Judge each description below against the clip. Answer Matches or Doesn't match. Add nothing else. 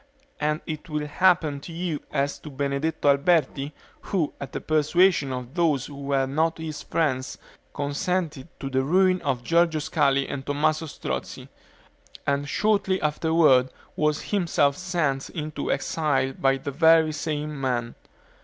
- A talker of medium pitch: Matches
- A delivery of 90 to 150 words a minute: Matches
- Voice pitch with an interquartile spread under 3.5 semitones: Matches